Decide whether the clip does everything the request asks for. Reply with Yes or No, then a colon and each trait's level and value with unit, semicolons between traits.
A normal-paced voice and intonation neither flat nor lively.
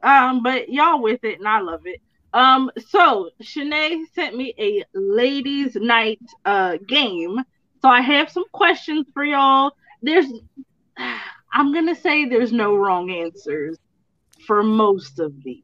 No: average, 145 wpm; wide, 6.1 semitones